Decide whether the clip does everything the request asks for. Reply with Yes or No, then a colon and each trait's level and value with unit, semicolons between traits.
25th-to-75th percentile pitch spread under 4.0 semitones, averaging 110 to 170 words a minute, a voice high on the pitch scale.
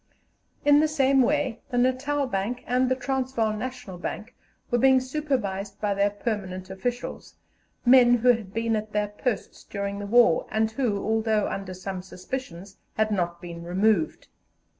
No: average, 4.4 semitones; average, 160 wpm; high, 220 Hz